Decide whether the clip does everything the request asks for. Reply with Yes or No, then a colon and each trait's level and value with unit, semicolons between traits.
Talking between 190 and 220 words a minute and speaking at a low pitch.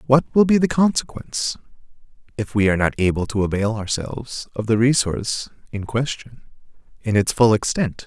No: average, 165 wpm; low, 115 Hz